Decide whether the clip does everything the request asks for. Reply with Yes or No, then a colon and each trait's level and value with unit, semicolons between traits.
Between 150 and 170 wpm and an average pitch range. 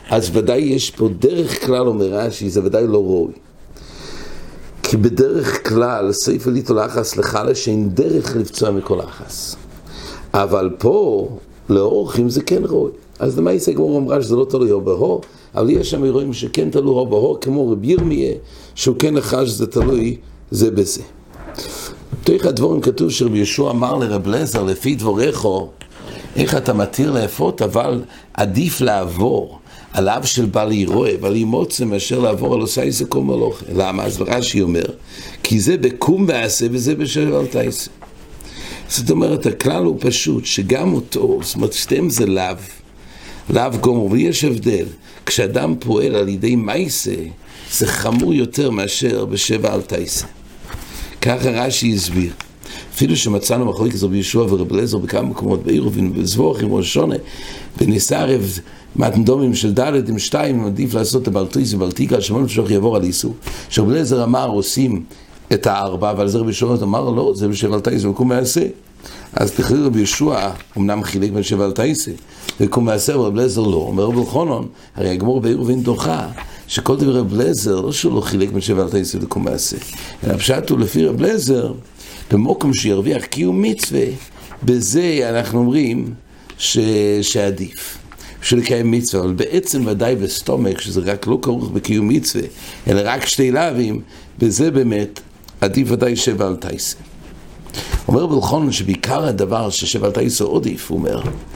Yes: average, 155 wpm; average, 4.3 semitones